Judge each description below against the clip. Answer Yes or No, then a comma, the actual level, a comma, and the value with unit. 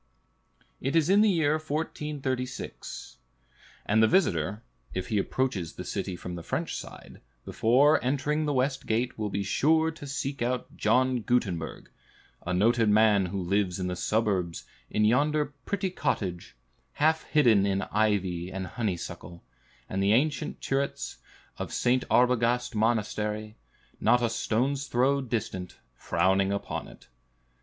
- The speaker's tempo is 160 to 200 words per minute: No, average, 140 wpm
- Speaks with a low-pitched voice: Yes, low, 115 Hz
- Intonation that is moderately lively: No, wide, 5.9 semitones